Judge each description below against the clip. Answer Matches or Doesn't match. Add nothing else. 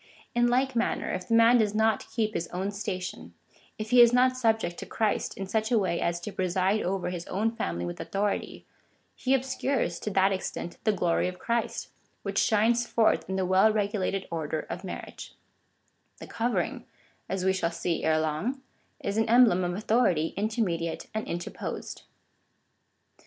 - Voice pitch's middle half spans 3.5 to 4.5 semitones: Matches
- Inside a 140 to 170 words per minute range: Doesn't match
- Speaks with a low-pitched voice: Doesn't match